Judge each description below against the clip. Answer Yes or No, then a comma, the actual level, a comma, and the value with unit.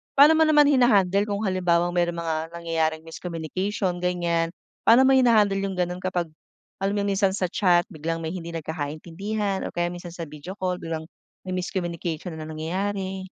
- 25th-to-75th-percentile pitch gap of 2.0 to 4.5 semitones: Yes, average, 3.0 semitones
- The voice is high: No, medium, 180 Hz